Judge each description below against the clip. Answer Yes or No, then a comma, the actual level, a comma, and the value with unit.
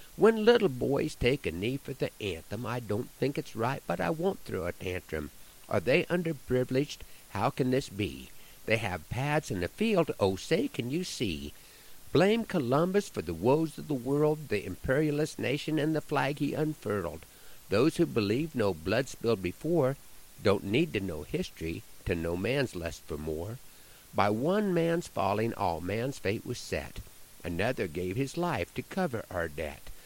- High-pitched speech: No, low, 130 Hz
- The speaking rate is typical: Yes, average, 180 wpm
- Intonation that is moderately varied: No, wide, 8.6 semitones